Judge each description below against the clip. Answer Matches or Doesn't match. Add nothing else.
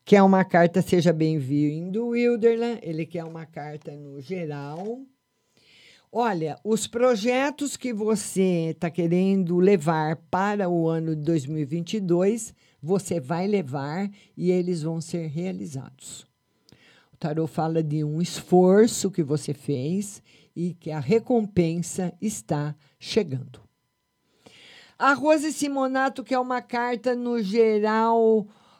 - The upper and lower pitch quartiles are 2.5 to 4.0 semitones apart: Doesn't match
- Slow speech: Matches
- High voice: Doesn't match